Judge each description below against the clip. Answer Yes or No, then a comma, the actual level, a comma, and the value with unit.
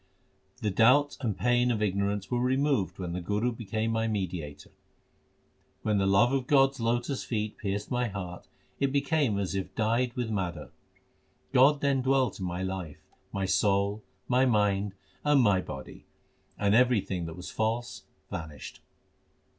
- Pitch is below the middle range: Yes, low, 110 Hz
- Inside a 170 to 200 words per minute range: No, average, 155 wpm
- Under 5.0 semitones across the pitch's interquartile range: Yes, average, 4.4 semitones